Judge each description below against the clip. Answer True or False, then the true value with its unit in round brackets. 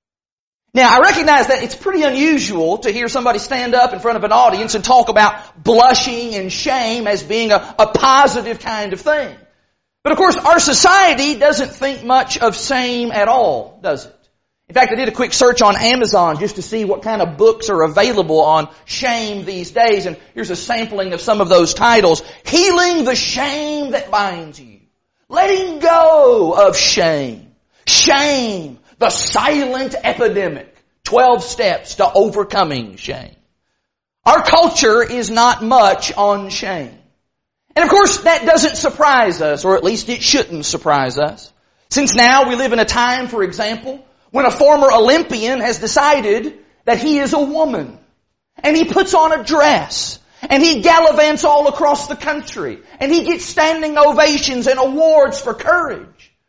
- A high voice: True (255 Hz)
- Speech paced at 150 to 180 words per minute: True (170 wpm)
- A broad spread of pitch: True (5.7 semitones)